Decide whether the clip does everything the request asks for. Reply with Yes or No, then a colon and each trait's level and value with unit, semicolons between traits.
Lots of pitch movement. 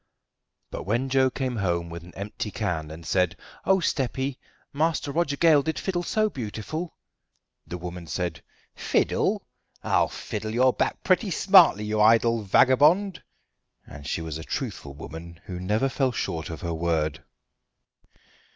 Yes: wide, 8.7 semitones